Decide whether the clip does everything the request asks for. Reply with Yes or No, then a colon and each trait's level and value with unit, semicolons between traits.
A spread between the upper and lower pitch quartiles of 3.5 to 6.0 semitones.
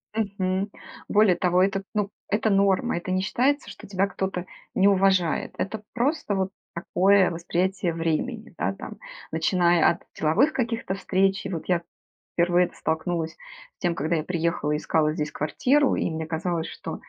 No: average, 2.9 semitones